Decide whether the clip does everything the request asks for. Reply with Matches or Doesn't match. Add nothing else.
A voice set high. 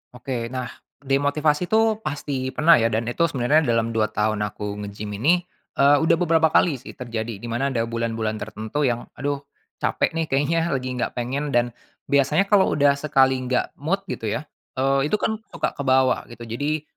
Doesn't match